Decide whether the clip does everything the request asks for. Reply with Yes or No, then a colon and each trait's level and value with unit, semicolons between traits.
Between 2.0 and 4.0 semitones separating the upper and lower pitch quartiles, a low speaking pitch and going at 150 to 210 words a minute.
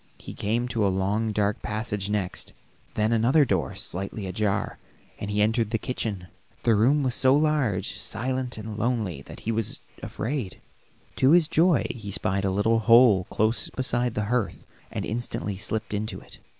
Yes: average, 3.2 semitones; low, 110 Hz; average, 170 wpm